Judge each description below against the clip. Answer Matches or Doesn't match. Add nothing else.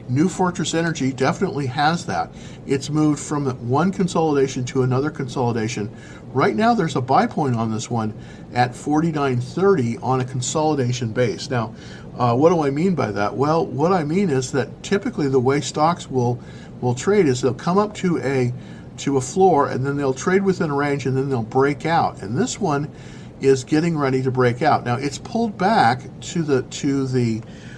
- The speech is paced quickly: Doesn't match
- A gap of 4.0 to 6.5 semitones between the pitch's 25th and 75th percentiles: Matches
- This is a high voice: Doesn't match